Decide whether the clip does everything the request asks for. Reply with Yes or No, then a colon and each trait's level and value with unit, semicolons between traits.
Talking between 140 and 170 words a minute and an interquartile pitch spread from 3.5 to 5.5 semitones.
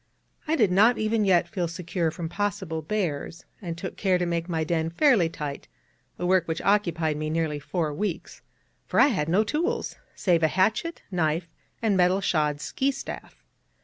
No: average, 180 wpm; average, 4.2 semitones